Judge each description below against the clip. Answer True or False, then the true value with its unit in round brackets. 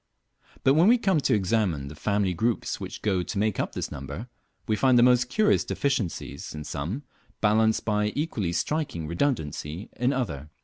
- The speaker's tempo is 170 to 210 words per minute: True (175 wpm)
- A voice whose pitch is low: True (105 Hz)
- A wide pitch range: True (7.0 semitones)